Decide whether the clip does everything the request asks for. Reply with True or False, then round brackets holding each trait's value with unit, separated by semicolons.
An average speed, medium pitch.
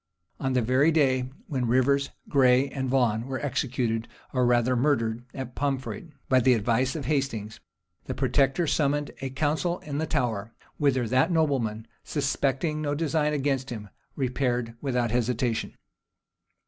False (145 wpm; 130 Hz)